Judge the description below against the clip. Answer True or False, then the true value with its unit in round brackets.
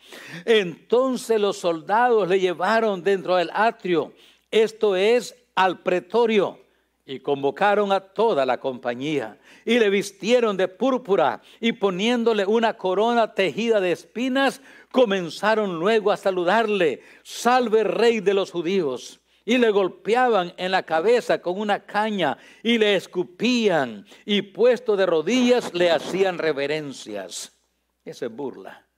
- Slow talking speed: True (125 wpm)